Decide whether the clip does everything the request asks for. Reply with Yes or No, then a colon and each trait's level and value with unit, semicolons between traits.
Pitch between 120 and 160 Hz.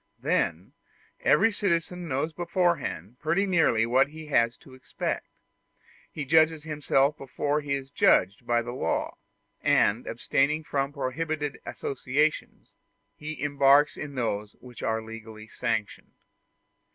Yes: medium, 140 Hz